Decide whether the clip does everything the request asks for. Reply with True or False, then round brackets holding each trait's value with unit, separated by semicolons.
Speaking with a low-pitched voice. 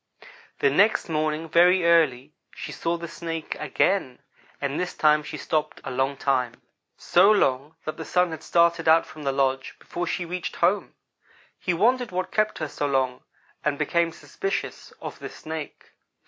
False (160 Hz)